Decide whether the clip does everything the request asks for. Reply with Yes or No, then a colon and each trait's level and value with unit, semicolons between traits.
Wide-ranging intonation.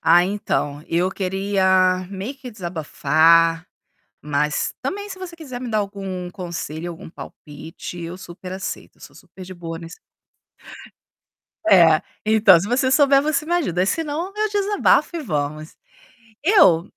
Yes: wide, 7.7 semitones